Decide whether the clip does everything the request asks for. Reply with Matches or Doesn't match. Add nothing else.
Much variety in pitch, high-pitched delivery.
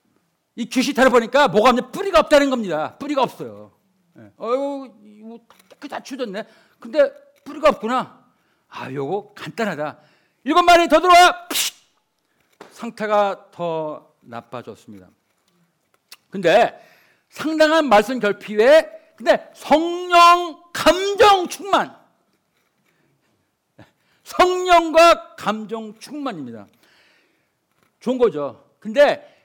Matches